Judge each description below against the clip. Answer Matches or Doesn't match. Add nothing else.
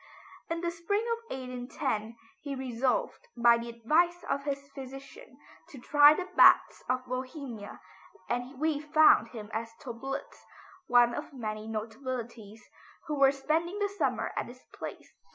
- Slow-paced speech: Doesn't match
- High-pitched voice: Matches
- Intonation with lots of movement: Doesn't match